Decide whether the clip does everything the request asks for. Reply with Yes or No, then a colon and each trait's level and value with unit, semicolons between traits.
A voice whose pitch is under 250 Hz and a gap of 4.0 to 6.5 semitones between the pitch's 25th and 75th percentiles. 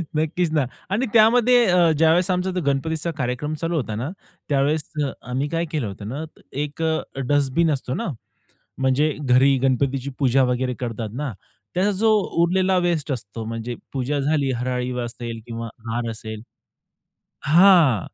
Yes: medium, 140 Hz; average, 4.8 semitones